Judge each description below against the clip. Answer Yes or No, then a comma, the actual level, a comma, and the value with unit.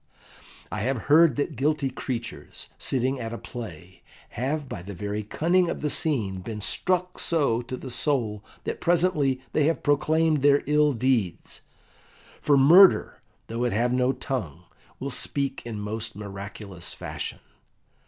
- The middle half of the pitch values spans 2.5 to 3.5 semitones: No, wide, 5.6 semitones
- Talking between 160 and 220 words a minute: No, average, 150 wpm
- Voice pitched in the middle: No, low, 130 Hz